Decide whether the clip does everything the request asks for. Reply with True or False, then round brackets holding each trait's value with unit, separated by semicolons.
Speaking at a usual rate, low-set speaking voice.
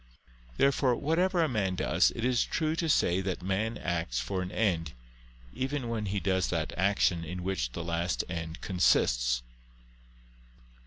True (155 wpm; 95 Hz)